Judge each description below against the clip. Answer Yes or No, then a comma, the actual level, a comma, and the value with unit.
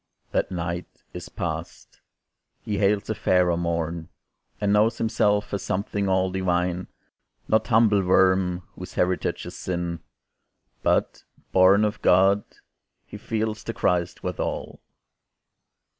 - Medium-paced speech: No, slow, 120 wpm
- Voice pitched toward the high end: No, very low, 95 Hz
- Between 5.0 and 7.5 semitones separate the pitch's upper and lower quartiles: No, narrow, 2.5 semitones